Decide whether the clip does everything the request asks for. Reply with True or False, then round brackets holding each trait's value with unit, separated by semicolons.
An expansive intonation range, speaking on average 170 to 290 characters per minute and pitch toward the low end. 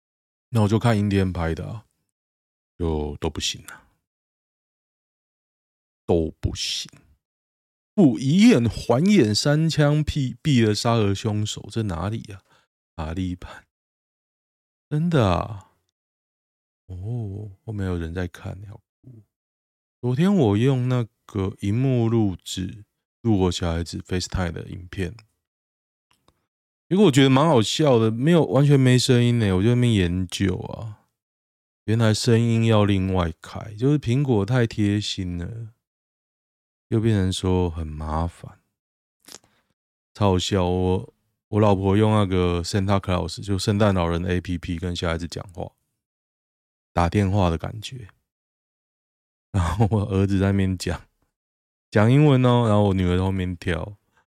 False (4.6 semitones; 210 characters per minute; 100 Hz)